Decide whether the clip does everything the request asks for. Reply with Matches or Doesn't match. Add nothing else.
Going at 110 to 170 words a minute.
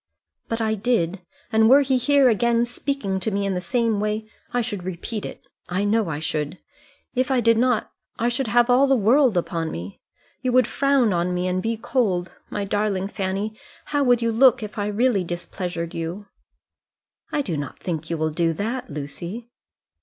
Doesn't match